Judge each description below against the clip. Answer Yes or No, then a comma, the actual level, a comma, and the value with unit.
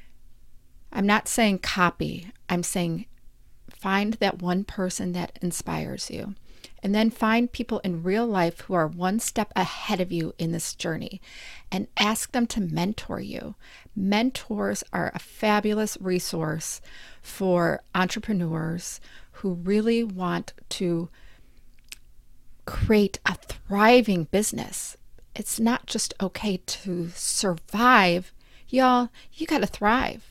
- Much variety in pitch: No, average, 3.8 semitones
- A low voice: No, high, 195 Hz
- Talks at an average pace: No, slow, 125 wpm